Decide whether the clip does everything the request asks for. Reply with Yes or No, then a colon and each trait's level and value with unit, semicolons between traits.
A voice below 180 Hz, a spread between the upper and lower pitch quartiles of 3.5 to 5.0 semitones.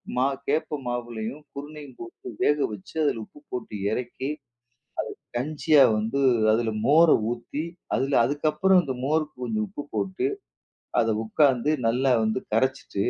Yes: low, 135 Hz; average, 4.0 semitones